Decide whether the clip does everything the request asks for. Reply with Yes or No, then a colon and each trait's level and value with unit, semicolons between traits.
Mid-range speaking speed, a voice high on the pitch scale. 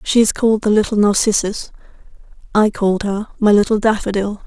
Yes: average, 160 wpm; high, 210 Hz